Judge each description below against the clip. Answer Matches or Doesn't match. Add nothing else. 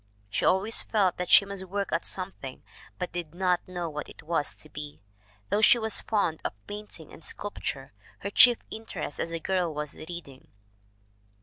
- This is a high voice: Doesn't match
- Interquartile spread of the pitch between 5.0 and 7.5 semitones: Doesn't match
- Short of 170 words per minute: Doesn't match